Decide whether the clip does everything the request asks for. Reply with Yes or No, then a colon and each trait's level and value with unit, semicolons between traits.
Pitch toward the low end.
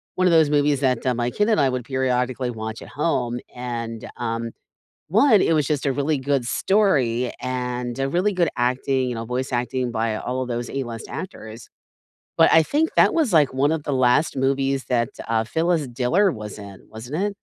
Yes: low, 130 Hz